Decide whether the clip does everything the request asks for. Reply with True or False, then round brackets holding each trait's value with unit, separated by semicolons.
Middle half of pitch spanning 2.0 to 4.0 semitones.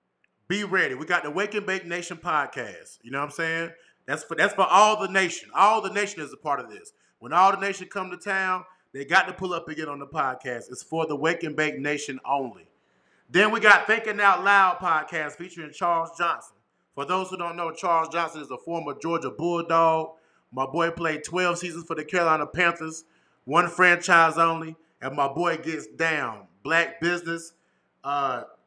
True (2.8 semitones)